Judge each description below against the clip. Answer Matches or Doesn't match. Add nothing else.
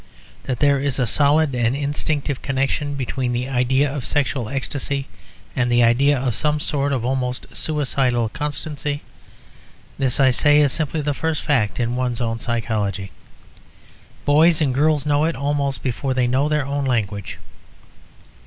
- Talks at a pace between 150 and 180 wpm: Matches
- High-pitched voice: Doesn't match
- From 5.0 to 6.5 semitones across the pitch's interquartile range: Doesn't match